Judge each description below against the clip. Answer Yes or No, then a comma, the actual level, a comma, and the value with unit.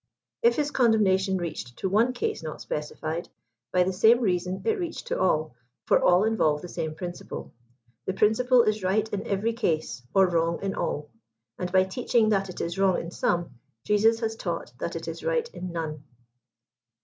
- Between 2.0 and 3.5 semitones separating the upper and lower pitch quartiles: No, average, 4.6 semitones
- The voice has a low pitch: No, high, 190 Hz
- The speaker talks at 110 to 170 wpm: No, average, 185 wpm